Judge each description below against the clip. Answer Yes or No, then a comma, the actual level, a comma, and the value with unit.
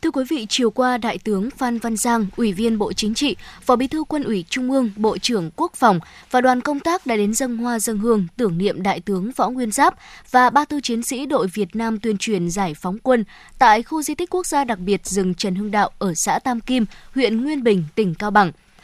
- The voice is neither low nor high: No, high, 230 Hz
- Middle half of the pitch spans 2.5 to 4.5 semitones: Yes, average, 3.9 semitones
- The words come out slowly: No, fast, 250 wpm